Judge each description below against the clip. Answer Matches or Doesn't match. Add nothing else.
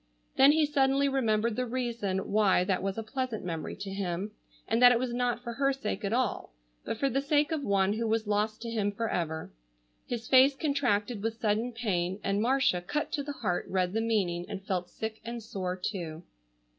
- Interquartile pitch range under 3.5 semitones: Doesn't match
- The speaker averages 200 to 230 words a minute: Matches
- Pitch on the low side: Doesn't match